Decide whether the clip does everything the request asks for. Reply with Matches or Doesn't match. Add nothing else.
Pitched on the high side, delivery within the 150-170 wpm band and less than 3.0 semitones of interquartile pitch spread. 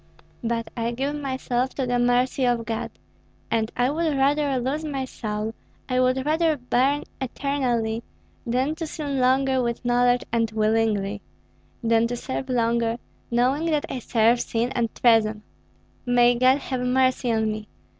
Matches